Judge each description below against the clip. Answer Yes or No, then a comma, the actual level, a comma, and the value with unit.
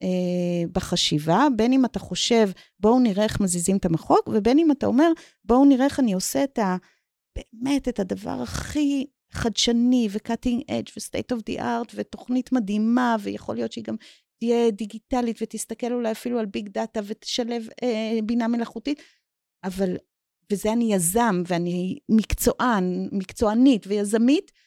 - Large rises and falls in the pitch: No, average, 4.0 semitones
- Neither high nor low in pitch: No, high, 225 Hz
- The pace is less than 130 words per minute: No, average, 145 wpm